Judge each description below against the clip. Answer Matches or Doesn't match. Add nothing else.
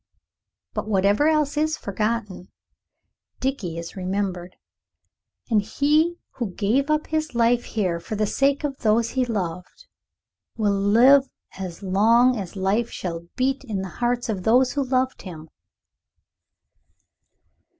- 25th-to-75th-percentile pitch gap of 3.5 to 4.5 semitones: Doesn't match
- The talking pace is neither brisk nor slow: Doesn't match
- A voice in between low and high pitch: Doesn't match